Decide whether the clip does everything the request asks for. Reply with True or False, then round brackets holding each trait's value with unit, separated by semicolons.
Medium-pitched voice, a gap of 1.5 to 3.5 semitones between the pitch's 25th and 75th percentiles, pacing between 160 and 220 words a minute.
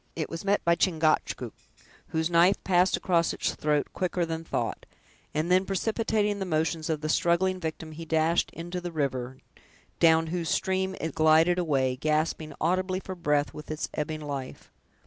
True (165 Hz; 2.7 semitones; 165 wpm)